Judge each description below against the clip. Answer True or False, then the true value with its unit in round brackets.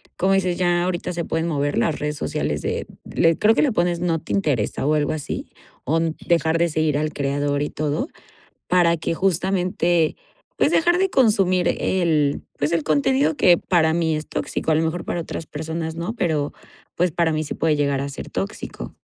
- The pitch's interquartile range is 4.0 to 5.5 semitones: False (2.9 semitones)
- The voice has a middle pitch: True (165 Hz)